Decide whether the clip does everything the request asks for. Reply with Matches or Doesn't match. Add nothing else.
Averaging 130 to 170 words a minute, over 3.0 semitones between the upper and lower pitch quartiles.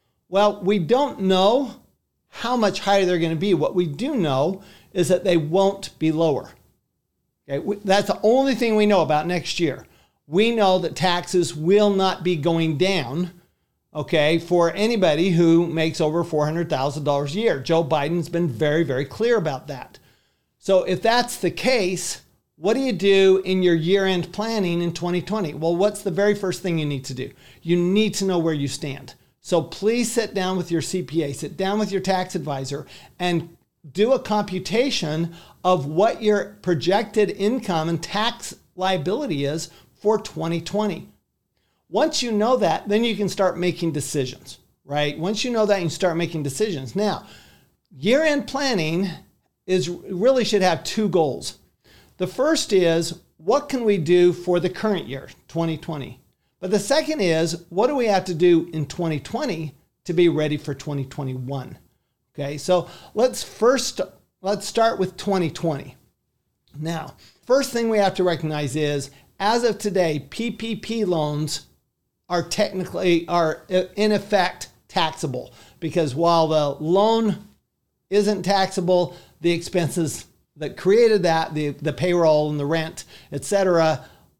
Matches